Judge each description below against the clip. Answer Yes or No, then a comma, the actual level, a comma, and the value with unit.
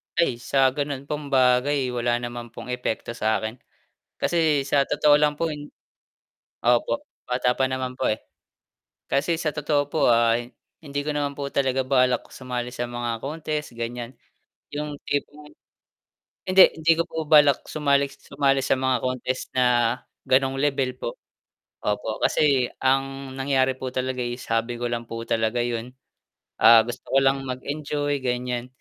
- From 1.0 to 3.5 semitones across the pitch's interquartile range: Yes, average, 2.8 semitones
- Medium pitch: No, low, 130 Hz